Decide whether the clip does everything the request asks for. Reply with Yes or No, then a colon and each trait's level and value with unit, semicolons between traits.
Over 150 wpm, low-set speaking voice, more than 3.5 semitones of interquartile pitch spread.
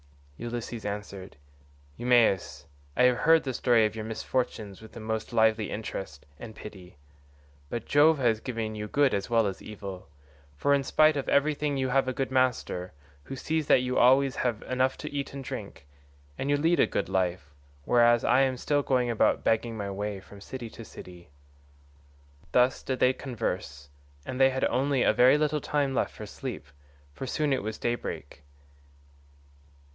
Yes: average, 175 wpm; low, 120 Hz; average, 3.9 semitones